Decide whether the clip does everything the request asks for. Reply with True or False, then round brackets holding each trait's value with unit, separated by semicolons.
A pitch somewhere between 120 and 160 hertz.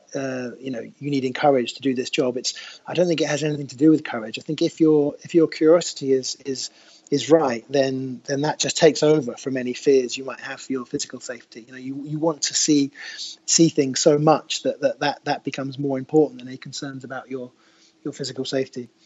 True (140 Hz)